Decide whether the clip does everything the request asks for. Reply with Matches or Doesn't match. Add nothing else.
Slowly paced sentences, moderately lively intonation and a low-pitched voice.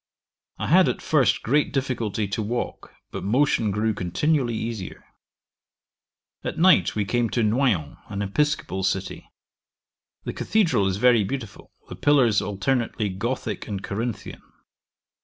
Matches